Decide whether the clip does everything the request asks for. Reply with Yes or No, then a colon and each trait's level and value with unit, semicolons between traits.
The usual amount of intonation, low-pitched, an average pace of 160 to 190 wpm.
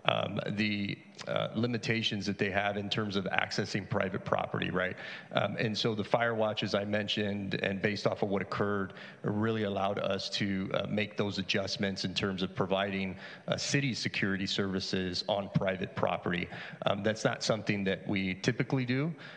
No: narrow, 2.1 semitones; low, 100 Hz; average, 170 wpm